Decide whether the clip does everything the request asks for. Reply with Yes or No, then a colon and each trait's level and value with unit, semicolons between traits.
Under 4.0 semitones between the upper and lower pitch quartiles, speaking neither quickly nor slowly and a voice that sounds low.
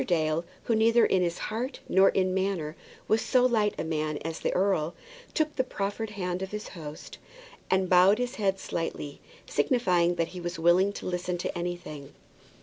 No: average, 3.6 semitones; average, 175 wpm; medium, 185 Hz